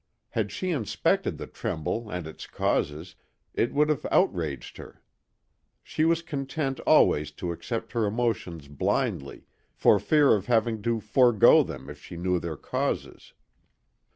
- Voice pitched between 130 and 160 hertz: No, low, 110 Hz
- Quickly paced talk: No, average, 145 wpm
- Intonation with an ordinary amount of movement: No, wide, 8.1 semitones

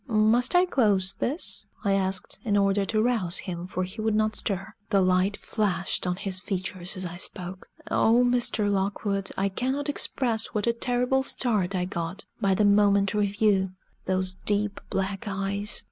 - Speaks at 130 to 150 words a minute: No, average, 170 wpm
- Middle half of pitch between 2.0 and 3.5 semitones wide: Yes, average, 2.7 semitones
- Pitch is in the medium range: No, high, 200 Hz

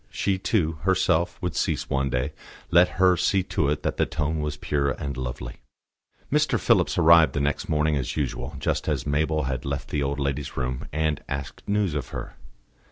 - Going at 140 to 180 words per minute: No, average, 190 wpm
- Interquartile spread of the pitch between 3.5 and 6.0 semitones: No, average, 2.7 semitones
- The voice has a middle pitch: No, very low, 75 Hz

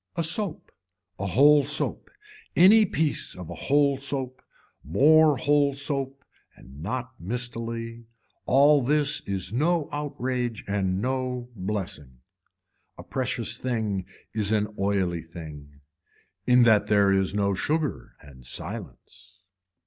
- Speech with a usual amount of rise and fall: No, wide, 6.5 semitones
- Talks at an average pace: No, slow, 120 wpm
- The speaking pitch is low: Yes, low, 115 Hz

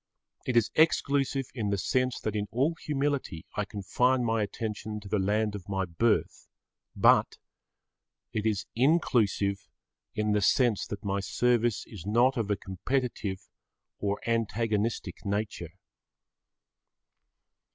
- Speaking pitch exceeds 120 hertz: No, low, 110 Hz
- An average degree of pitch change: Yes, average, 3.5 semitones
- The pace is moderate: No, slow, 130 wpm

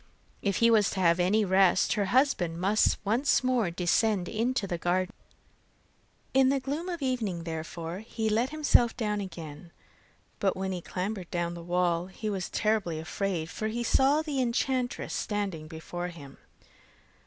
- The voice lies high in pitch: Yes, high, 195 Hz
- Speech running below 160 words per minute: No, average, 165 wpm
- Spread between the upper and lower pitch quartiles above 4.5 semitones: Yes, average, 5.1 semitones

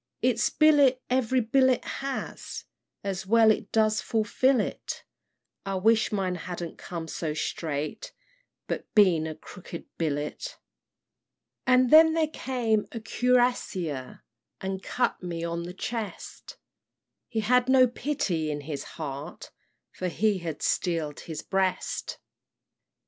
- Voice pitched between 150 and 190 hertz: No, high, 205 Hz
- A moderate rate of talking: No, slow, 125 wpm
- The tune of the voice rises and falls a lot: Yes, wide, 6.8 semitones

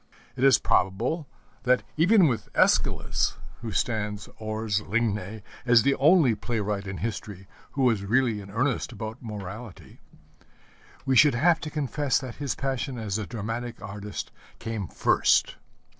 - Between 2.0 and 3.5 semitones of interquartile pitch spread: No, average, 4.1 semitones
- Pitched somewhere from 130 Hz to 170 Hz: No, low, 115 Hz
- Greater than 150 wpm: No, average, 145 wpm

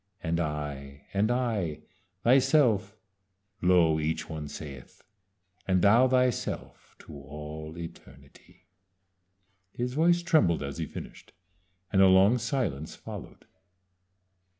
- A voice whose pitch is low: Yes, very low, 90 Hz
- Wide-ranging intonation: Yes, wide, 8.0 semitones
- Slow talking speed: Yes, slow, 105 wpm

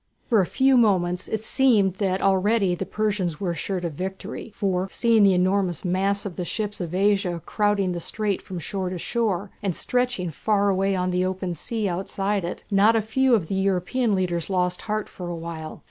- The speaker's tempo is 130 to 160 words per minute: No, average, 200 wpm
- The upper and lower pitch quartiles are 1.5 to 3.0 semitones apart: Yes, narrow, 2.6 semitones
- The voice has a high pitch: Yes, high, 195 Hz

